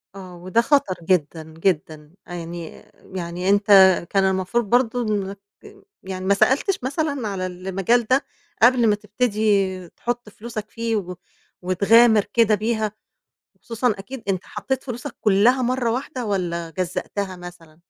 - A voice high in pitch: Yes, high, 205 Hz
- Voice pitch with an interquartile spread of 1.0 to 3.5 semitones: No, average, 4.3 semitones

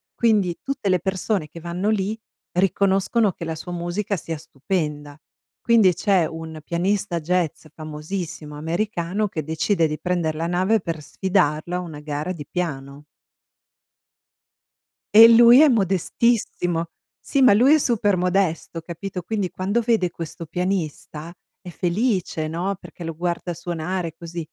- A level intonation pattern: No, average, 3.5 semitones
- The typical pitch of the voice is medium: Yes, medium, 175 Hz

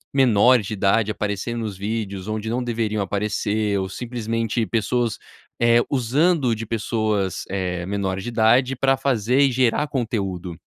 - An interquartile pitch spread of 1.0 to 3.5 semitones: Yes, average, 3.2 semitones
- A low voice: Yes, low, 110 Hz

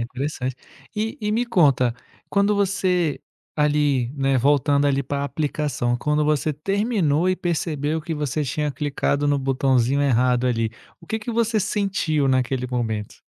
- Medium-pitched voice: Yes, medium, 145 Hz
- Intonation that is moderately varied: Yes, average, 4.9 semitones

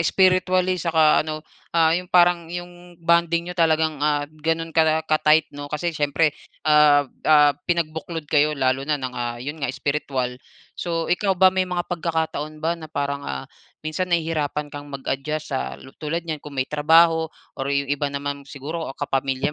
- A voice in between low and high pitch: Yes, medium, 155 Hz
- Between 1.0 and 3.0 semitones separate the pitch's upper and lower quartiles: Yes, average, 2.7 semitones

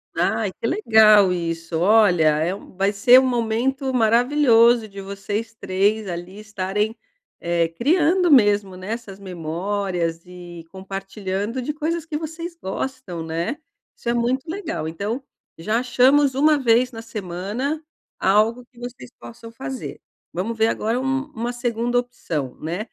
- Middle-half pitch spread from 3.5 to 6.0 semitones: Yes, average, 5.2 semitones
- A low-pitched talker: No, high, 220 Hz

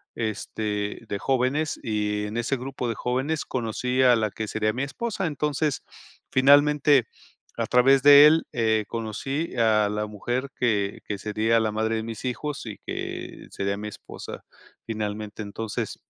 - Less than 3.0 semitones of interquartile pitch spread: No, average, 4.1 semitones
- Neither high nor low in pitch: No, low, 115 Hz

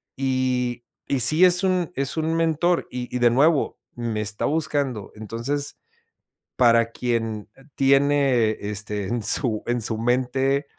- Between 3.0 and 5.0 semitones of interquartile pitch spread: Yes, average, 3.7 semitones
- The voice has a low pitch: Yes, low, 125 Hz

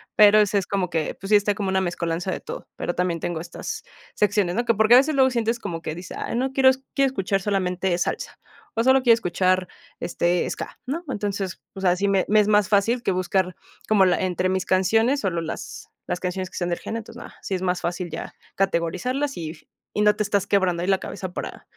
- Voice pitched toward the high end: Yes, high, 195 Hz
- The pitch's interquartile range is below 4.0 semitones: Yes, average, 3.0 semitones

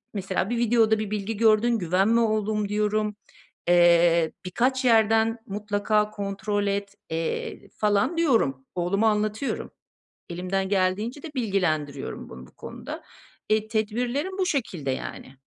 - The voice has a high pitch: Yes, high, 210 Hz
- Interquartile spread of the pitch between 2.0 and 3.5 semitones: Yes, average, 3.1 semitones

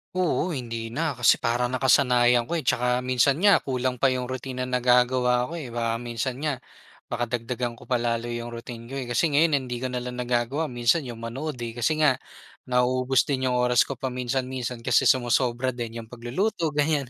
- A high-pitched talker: No, low, 125 Hz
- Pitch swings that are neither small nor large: No, narrow, 1.7 semitones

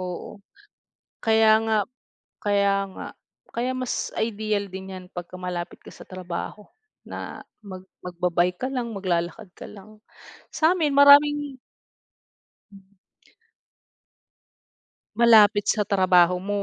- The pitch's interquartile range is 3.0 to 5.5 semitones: Yes, average, 3.4 semitones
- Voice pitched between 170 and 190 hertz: No, high, 205 Hz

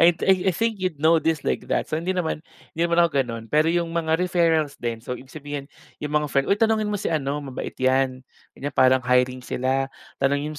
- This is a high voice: No, medium, 150 Hz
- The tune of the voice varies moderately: Yes, average, 4.2 semitones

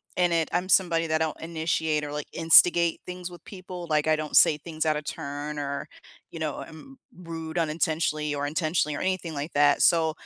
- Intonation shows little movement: Yes, narrow, 2.1 semitones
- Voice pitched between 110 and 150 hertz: No, medium, 160 Hz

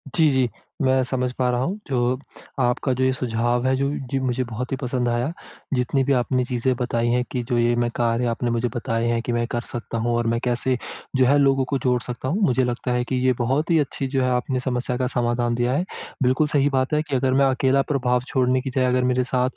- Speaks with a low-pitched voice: Yes, low, 125 Hz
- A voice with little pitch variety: Yes, narrow, 1.4 semitones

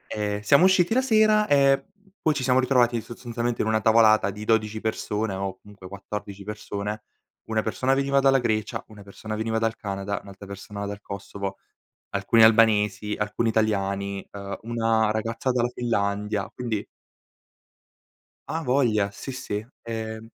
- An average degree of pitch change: Yes, average, 3.0 semitones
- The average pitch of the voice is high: No, low, 110 Hz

